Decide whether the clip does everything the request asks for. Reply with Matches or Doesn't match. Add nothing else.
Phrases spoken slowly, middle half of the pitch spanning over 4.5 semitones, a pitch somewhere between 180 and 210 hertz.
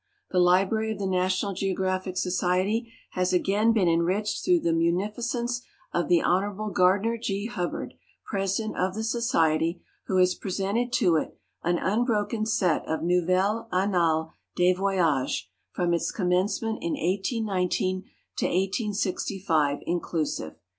Doesn't match